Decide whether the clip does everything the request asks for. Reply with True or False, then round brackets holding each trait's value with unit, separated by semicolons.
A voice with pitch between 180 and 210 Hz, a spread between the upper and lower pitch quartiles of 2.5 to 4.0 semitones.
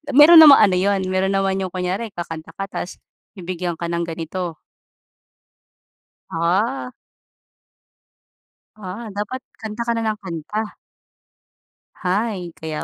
True (190 Hz; 3.7 semitones)